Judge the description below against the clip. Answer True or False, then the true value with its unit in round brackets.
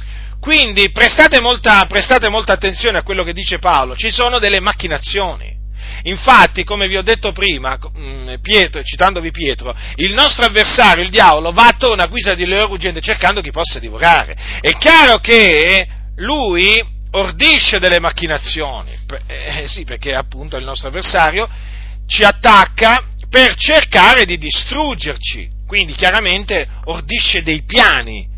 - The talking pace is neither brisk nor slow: True (135 wpm)